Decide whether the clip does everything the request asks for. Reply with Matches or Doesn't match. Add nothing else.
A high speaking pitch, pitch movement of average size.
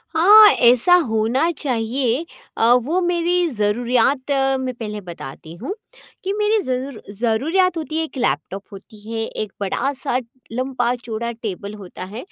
Doesn't match